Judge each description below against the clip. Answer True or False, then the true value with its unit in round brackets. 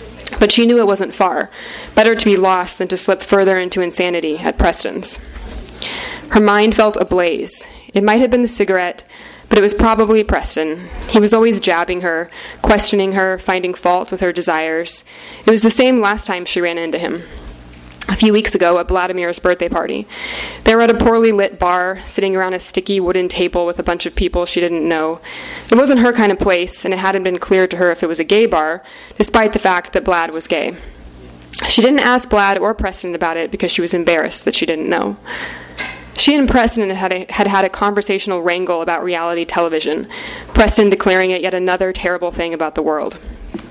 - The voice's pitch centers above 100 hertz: True (185 Hz)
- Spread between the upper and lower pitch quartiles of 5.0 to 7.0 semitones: False (3.2 semitones)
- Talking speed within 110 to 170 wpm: False (205 wpm)